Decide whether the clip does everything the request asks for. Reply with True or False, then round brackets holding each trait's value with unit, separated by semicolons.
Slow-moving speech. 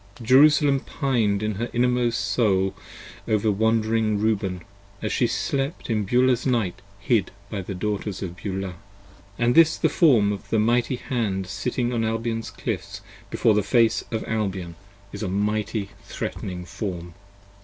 False (155 wpm)